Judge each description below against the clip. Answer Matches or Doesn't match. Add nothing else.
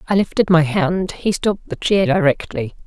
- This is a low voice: Doesn't match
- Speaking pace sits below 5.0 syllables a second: Doesn't match